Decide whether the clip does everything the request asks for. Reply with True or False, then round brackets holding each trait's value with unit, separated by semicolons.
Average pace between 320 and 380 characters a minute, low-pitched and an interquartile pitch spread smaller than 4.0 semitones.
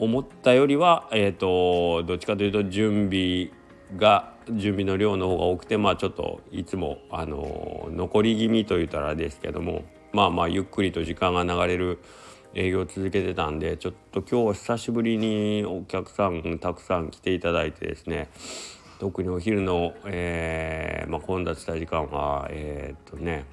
True (330 characters per minute; 90 Hz; 3.6 semitones)